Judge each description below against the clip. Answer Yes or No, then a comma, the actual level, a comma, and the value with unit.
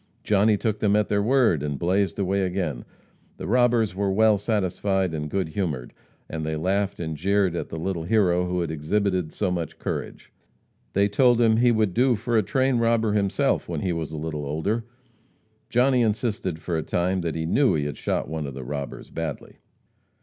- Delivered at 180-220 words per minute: Yes, average, 195 wpm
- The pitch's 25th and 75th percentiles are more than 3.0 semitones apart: Yes, average, 5.0 semitones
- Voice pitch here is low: Yes, very low, 95 Hz